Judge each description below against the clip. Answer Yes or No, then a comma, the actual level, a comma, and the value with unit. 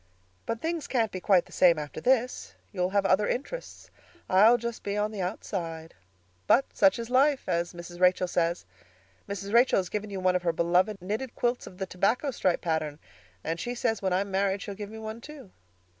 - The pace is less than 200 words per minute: No, fast, 205 wpm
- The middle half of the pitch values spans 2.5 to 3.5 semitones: No, average, 4.2 semitones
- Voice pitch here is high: Yes, high, 200 Hz